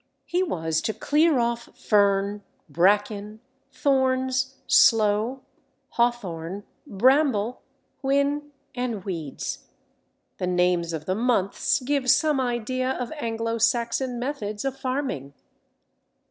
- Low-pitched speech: No, high, 235 Hz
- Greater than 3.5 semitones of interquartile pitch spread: Yes, average, 4.7 semitones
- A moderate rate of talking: No, slow, 105 wpm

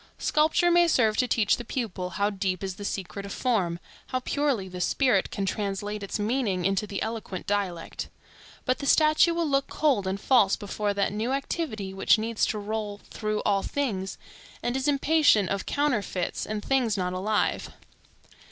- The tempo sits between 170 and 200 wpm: Yes, average, 175 wpm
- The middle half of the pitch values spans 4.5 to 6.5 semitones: Yes, average, 4.9 semitones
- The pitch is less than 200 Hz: No, high, 210 Hz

